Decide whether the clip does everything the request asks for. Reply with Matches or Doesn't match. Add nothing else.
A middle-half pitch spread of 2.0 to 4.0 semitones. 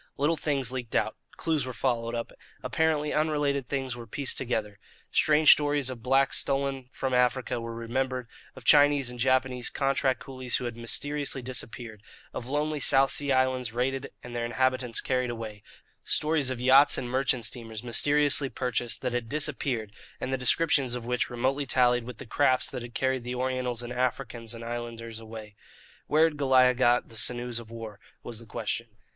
Matches